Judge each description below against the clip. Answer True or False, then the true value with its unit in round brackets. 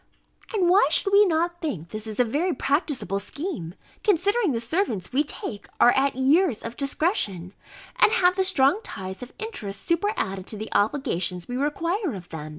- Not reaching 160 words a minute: False (170 wpm)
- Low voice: False (280 Hz)